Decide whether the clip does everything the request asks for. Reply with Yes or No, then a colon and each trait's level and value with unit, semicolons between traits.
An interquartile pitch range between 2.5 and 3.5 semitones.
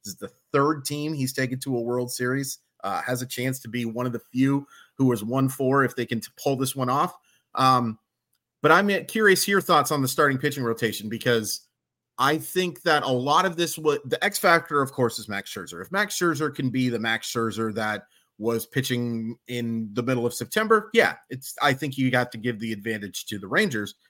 No: average, 4.1 semitones